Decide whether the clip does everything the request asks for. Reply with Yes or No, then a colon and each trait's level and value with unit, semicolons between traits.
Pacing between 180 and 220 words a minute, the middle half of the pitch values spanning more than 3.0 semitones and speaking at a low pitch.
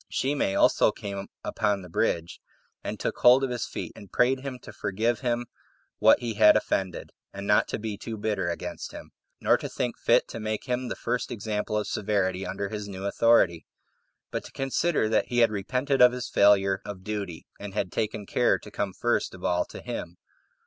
Yes: average, 200 wpm; average, 3.5 semitones; low, 105 Hz